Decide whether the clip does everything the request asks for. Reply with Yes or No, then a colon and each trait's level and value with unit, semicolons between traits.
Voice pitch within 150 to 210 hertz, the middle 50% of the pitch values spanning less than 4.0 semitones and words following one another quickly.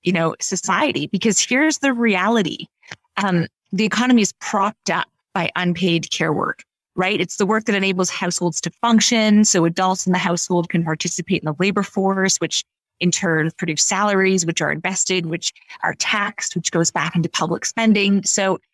No: medium, 185 Hz; average, 2.9 semitones; average, 175 wpm